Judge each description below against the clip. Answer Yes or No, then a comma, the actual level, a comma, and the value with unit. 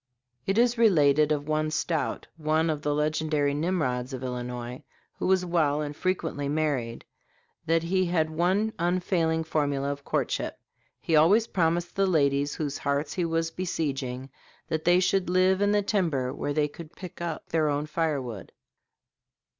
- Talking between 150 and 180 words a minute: Yes, average, 160 wpm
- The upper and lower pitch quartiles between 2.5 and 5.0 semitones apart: Yes, average, 3.5 semitones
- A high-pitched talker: No, medium, 155 Hz